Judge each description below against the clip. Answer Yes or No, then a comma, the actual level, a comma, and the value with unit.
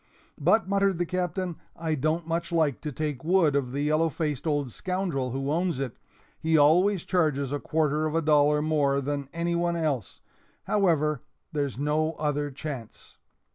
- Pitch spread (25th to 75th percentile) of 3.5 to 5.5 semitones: No, average, 2.8 semitones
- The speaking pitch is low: No, medium, 155 Hz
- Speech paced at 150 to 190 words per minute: Yes, average, 170 wpm